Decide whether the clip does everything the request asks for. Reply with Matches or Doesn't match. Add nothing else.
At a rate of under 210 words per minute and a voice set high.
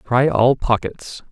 Doesn't match